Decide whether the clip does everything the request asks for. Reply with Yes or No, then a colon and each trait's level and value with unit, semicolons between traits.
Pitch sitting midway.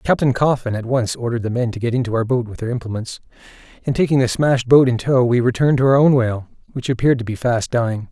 No: low, 125 Hz